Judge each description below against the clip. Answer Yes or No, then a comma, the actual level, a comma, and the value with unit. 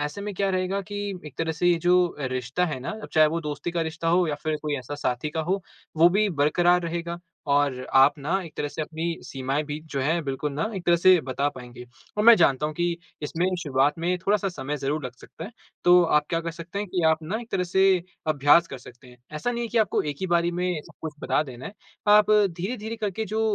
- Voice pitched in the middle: Yes, medium, 165 Hz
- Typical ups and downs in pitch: Yes, average, 3.8 semitones